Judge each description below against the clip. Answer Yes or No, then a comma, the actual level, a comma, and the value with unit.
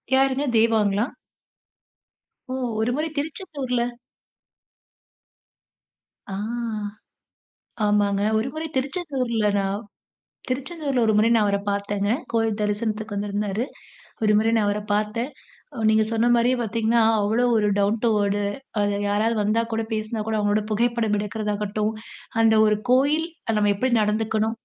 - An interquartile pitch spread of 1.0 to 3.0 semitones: Yes, narrow, 2.4 semitones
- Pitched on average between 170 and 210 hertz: No, high, 220 Hz